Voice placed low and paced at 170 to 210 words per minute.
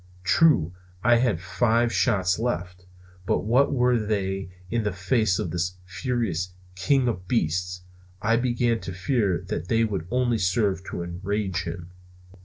No: low, 100 Hz; average, 150 wpm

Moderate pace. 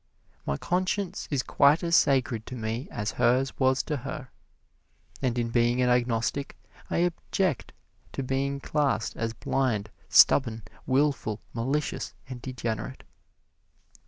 No: slow, 130 wpm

